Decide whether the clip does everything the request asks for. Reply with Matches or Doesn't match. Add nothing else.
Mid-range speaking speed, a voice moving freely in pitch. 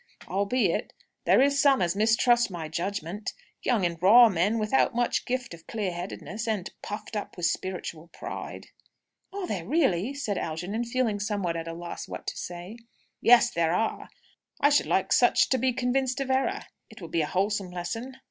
Matches